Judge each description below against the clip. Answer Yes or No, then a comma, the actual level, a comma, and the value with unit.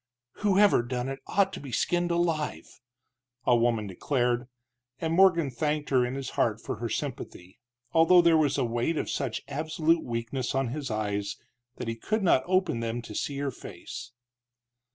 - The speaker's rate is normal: Yes, average, 175 wpm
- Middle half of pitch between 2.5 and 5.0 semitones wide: No, wide, 5.6 semitones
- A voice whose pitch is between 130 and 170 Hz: Yes, low, 135 Hz